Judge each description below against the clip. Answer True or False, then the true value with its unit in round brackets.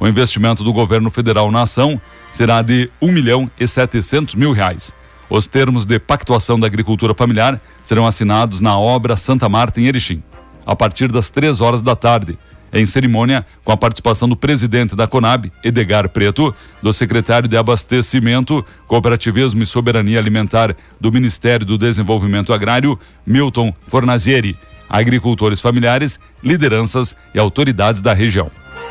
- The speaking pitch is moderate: False (115 Hz)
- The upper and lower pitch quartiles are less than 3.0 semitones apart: True (2.5 semitones)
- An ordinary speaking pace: True (145 wpm)